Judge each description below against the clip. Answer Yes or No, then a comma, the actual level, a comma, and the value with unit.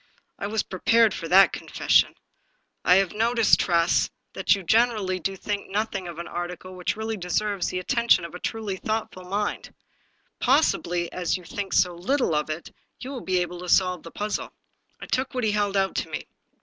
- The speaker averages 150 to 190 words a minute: No, average, 200 wpm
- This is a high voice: Yes, high, 195 Hz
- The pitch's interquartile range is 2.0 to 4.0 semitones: Yes, average, 3.4 semitones